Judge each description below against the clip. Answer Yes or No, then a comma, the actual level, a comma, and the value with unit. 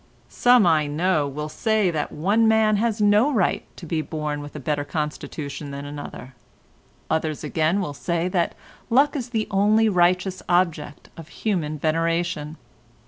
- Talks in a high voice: No, medium, 170 Hz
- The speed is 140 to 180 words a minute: Yes, average, 155 wpm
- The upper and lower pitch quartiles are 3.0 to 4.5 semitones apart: No, wide, 5.5 semitones